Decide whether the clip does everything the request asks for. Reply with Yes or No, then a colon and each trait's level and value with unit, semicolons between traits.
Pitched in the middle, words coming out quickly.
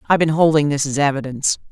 Yes: medium, 145 Hz; fast, 210 wpm